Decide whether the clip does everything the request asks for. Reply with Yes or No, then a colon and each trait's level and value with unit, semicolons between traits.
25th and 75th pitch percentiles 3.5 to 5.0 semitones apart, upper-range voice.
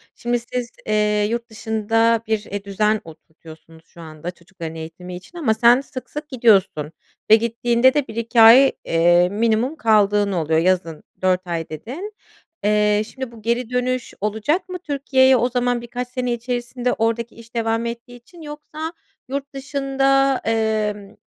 Yes: average, 3.8 semitones; high, 230 Hz